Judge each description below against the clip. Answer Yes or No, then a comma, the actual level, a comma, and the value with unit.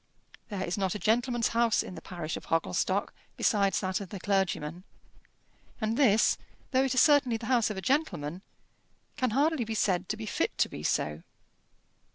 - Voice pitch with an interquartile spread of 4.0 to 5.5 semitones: Yes, average, 4.7 semitones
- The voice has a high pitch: Yes, high, 215 Hz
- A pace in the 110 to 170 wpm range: No, average, 185 wpm